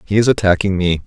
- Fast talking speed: Yes, fast, 225 wpm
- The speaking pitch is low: Yes, very low, 95 Hz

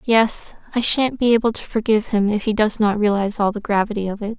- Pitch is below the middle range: No, high, 215 Hz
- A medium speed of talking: No, fast, 245 wpm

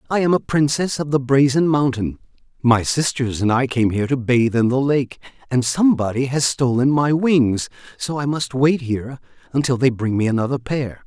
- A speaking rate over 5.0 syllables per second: Yes, 5.2 syllables/s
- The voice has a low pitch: Yes, low, 130 Hz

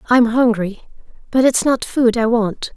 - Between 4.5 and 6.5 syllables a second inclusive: No, 4.2 syllables/s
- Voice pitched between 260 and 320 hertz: No, high, 235 Hz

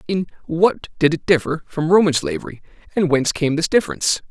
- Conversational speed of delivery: Yes, average, 180 wpm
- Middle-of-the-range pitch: Yes, medium, 165 Hz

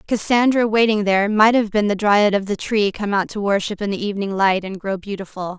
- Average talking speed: No, fast, 235 wpm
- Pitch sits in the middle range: No, high, 205 Hz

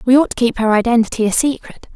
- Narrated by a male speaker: No, female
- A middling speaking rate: No, fast, 245 wpm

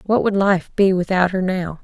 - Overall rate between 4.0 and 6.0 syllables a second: Yes, 4.7 syllables/s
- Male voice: No, female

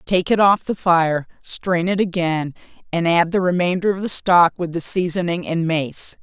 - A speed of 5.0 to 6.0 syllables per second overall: No, 4.5 syllables/s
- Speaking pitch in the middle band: Yes, medium, 175 Hz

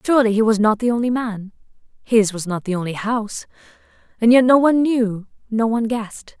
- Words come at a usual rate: Yes, average, 190 wpm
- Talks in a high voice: Yes, high, 225 Hz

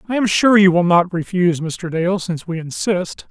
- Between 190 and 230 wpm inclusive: Yes, average, 200 wpm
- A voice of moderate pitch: Yes, medium, 180 Hz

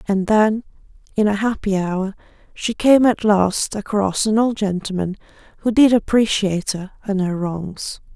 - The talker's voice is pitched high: Yes, high, 205 Hz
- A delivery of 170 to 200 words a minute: No, average, 155 wpm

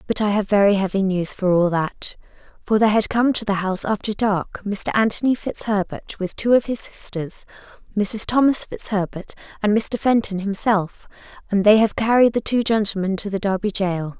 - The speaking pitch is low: No, high, 205 Hz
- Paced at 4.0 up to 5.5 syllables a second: Yes, 5.1 syllables/s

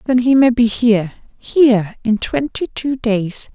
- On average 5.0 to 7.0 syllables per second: No, 4.2 syllables/s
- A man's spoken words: No, female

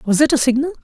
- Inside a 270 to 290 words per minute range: Yes, fast, 285 wpm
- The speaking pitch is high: Yes, very high, 270 Hz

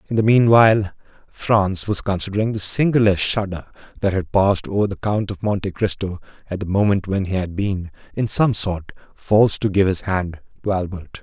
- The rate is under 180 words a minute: No, average, 185 wpm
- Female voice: No, male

